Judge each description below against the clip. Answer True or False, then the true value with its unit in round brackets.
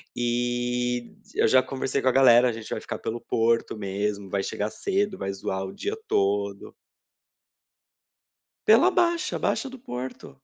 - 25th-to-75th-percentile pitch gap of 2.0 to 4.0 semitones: False (4.8 semitones)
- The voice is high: False (120 Hz)